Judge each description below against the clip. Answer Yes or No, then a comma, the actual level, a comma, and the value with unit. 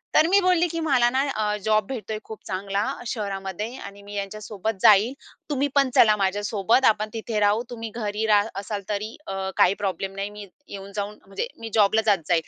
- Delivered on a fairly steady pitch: Yes, narrow, 2.2 semitones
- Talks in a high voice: Yes, high, 210 Hz